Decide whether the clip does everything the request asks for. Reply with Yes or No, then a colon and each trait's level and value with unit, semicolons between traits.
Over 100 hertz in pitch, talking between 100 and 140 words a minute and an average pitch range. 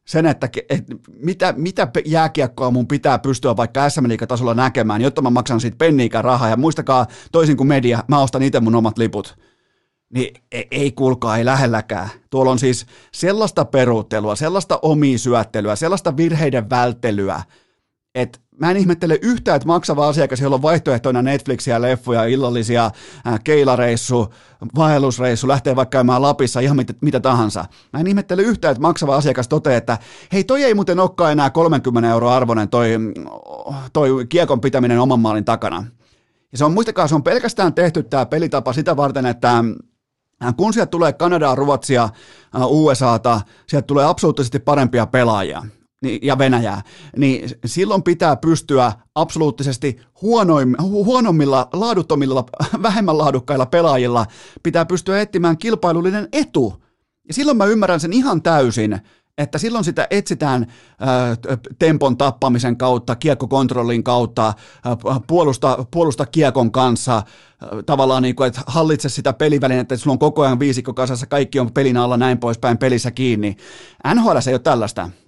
No: low, 135 Hz; average, 150 wpm; average, 4.5 semitones